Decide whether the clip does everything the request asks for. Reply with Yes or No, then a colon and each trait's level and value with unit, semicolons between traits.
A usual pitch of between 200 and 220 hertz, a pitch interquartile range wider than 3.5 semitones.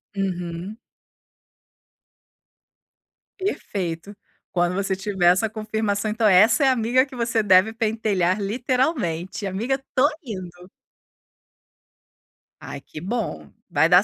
Yes: high, 205 Hz; average, 4.0 semitones